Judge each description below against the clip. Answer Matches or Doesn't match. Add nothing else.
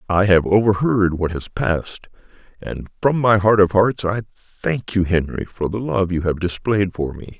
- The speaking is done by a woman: Doesn't match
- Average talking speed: Matches